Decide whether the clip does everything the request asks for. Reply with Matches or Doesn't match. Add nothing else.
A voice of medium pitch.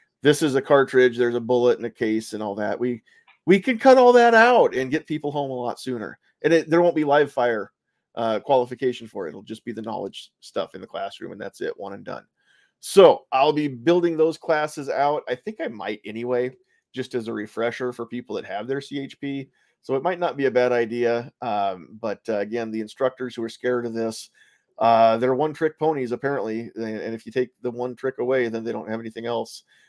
Doesn't match